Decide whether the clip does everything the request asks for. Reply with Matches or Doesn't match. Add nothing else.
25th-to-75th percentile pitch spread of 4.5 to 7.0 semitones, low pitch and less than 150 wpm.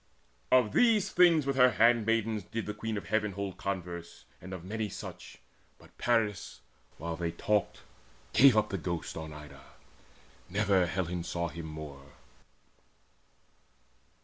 Matches